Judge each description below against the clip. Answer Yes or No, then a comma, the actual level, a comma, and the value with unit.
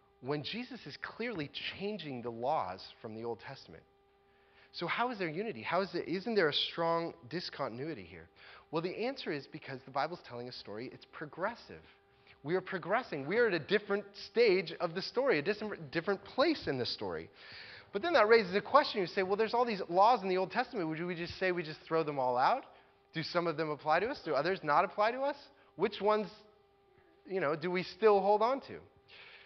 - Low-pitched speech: No, medium, 185 Hz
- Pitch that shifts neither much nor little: No, wide, 6.6 semitones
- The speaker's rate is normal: No, fast, 215 wpm